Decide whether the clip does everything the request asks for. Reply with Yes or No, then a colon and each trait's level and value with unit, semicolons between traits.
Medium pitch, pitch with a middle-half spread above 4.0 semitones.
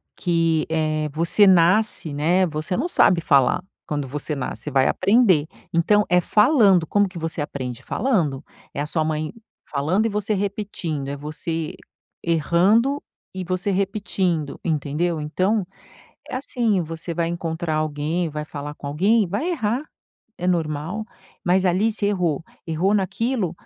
Yes: medium, 170 Hz; average, 4.7 semitones